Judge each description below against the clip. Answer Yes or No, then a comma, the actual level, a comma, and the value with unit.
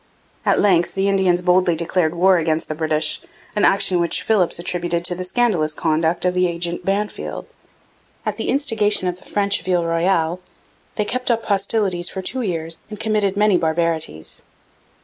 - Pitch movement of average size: Yes, average, 3.1 semitones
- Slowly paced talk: No, average, 170 wpm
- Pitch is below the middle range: No, medium, 180 Hz